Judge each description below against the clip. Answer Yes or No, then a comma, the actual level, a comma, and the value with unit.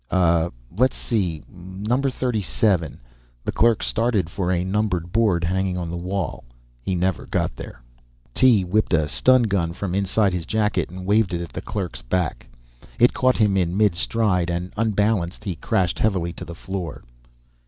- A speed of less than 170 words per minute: No, average, 175 wpm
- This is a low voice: Yes, very low, 95 Hz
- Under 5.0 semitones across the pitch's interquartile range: Yes, average, 3.7 semitones